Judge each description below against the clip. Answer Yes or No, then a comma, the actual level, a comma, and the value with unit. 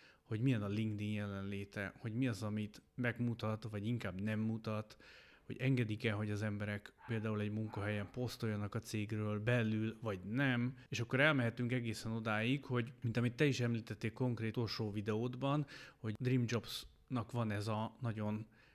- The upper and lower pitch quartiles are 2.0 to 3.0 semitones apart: Yes, narrow, 2.4 semitones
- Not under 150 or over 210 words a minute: Yes, fast, 155 wpm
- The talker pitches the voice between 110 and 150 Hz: Yes, low, 115 Hz